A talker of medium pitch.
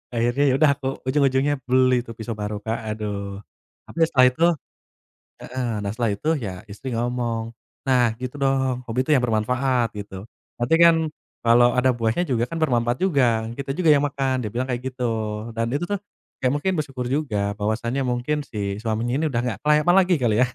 No: low, 125 Hz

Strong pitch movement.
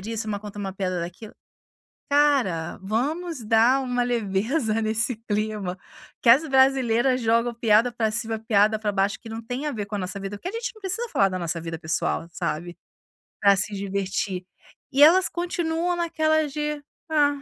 Yes: wide, 6.1 semitones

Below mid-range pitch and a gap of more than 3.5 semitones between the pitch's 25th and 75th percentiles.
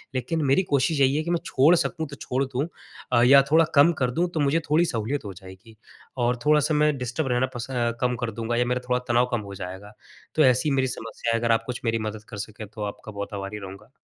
Yes: low, 125 Hz; average, 4.1 semitones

